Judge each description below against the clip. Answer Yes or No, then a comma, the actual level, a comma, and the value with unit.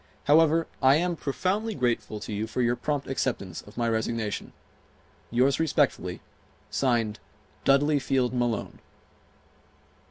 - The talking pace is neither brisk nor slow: No, slow, 120 wpm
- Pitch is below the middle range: Yes, low, 130 Hz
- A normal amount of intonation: Yes, average, 4.4 semitones